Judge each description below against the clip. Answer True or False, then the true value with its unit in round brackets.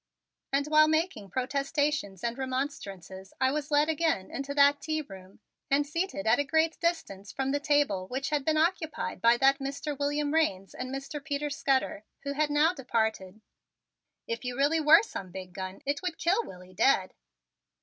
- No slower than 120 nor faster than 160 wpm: False (175 wpm)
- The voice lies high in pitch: True (280 Hz)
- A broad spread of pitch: False (4.8 semitones)